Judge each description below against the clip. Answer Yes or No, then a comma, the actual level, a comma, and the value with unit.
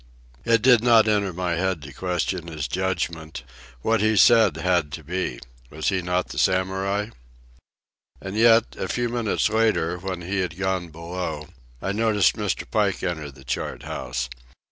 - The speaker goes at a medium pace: Yes, average, 165 wpm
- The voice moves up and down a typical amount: Yes, average, 3.9 semitones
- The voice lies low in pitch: Yes, very low, 95 Hz